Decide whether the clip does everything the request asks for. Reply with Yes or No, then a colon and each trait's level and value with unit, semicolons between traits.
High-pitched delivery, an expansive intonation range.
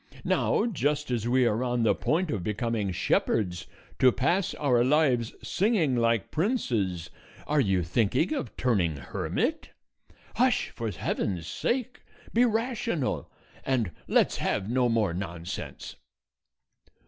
No: low, 120 Hz; wide, 7.2 semitones